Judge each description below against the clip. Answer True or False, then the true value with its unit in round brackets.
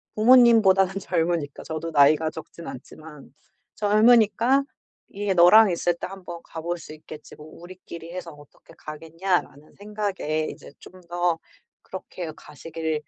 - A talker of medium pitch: True (170 Hz)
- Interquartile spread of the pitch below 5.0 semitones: True (3.7 semitones)